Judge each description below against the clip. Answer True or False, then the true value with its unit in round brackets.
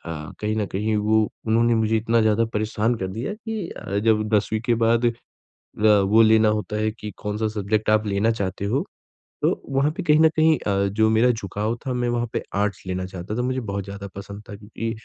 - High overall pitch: False (110 Hz)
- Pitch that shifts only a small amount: True (2.2 semitones)